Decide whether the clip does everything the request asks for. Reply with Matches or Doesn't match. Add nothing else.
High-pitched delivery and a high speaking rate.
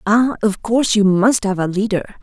Matches